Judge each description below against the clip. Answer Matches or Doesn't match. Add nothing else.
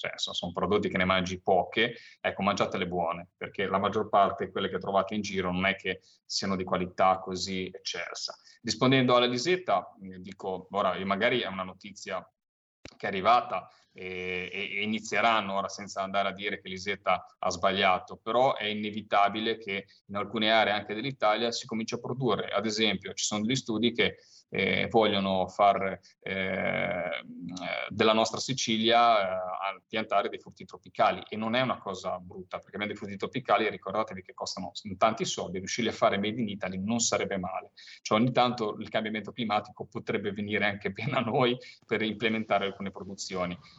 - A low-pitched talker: Matches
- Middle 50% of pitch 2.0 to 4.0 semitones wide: Matches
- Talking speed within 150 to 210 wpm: Matches